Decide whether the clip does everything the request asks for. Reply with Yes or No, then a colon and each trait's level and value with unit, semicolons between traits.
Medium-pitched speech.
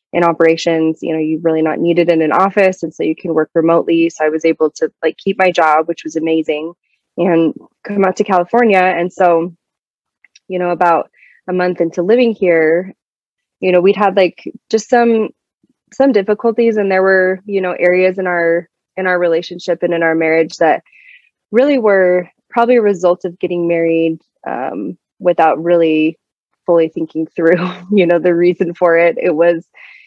Yes: medium, 175 Hz